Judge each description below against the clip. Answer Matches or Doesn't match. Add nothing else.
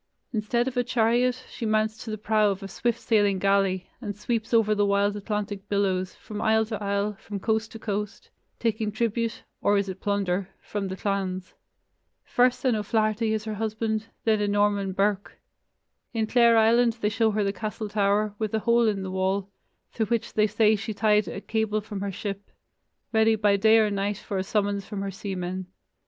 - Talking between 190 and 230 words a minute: Matches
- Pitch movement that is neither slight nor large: Doesn't match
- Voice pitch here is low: Doesn't match